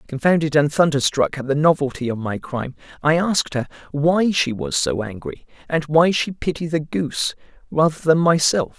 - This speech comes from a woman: No, male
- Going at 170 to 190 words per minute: Yes, average, 180 wpm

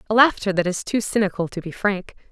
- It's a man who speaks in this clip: No, female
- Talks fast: Yes, fast, 235 wpm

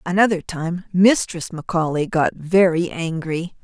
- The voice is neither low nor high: Yes, medium, 170 Hz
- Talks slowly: Yes, slow, 115 wpm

